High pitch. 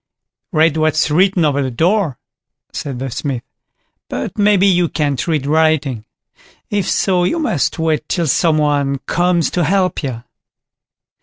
No: medium, 160 Hz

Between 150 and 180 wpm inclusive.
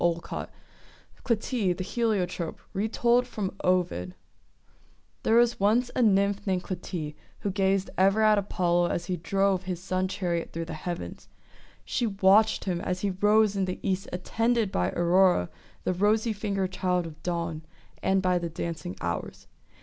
Yes: average, 155 wpm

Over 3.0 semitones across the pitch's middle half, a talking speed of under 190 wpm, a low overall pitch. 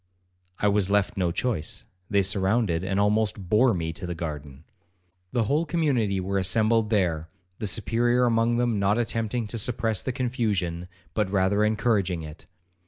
Yes: average, 3.7 semitones; average, 160 wpm; low, 105 Hz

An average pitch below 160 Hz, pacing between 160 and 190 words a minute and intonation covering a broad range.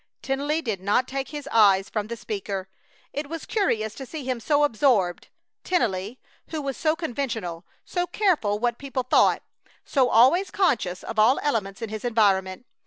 No: high, 240 Hz; average, 170 wpm; wide, 5.9 semitones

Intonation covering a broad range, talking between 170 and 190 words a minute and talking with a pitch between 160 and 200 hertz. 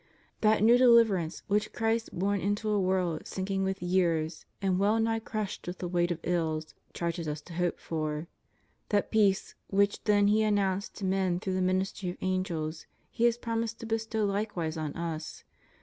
No: average, 3.6 semitones; average, 180 wpm; high, 190 Hz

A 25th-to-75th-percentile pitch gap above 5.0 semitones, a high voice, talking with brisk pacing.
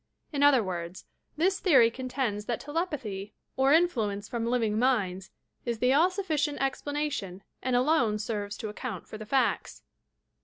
No: wide, 5.6 semitones; high, 245 Hz; average, 155 wpm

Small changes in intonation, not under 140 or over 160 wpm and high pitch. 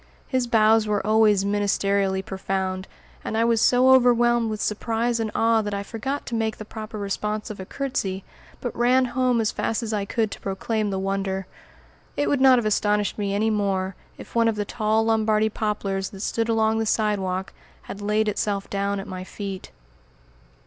No: narrow, 2.3 semitones; average, 190 wpm; high, 215 Hz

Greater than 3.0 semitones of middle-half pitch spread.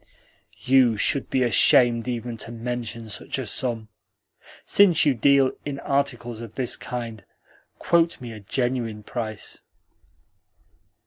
No: average, 2.7 semitones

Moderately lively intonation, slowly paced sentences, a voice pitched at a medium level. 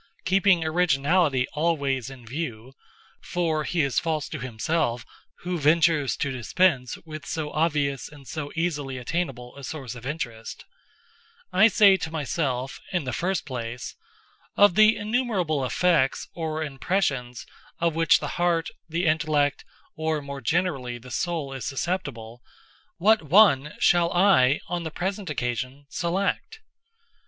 Yes: average, 4.7 semitones; slow, 130 wpm; medium, 155 Hz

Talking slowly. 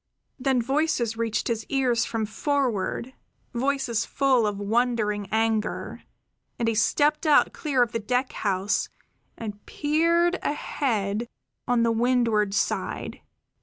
Yes: slow, 125 wpm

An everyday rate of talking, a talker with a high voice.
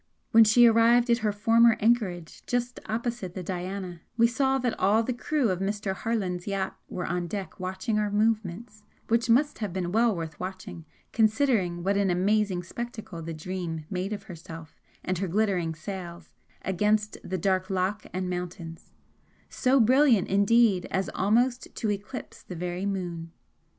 Yes: average, 160 wpm; high, 200 Hz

